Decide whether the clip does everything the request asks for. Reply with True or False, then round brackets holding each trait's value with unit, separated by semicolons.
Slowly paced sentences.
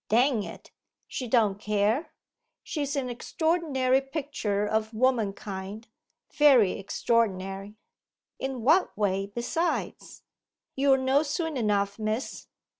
True (105 wpm)